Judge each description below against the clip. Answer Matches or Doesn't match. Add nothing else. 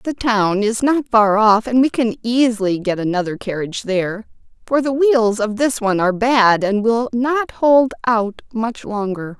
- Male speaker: Doesn't match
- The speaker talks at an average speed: Matches